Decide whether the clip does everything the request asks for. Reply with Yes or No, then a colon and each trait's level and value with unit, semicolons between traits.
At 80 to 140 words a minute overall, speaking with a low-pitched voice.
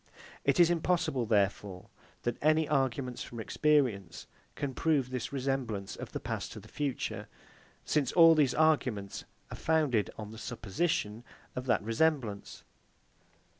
Yes: slow, 135 wpm; low, 130 Hz